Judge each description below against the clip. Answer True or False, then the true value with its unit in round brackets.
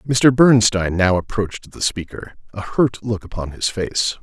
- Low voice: True (105 Hz)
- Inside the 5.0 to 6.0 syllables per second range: False (4.8 syllables/s)